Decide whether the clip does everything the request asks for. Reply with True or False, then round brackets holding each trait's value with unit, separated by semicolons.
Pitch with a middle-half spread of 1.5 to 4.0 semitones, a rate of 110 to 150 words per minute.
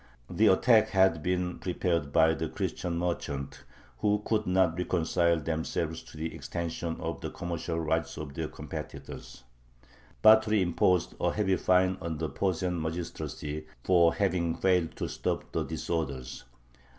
True (2.4 semitones; 140 wpm)